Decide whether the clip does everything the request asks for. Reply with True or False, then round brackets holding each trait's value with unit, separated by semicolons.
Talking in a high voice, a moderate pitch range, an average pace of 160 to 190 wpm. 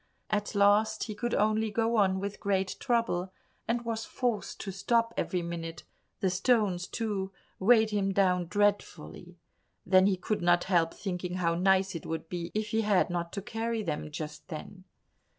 True (195 Hz; 3.3 semitones; 170 wpm)